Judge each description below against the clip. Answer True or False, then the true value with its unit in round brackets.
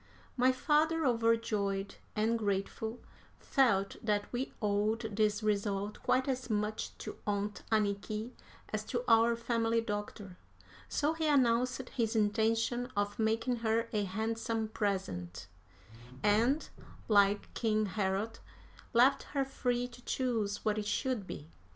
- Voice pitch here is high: True (220 Hz)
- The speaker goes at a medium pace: False (125 wpm)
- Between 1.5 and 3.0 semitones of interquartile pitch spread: True (2.7 semitones)